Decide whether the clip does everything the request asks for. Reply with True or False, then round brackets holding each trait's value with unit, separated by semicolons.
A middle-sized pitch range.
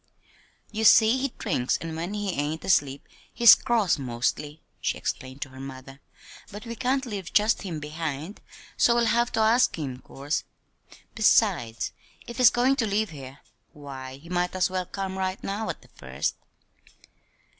False (7.6 semitones)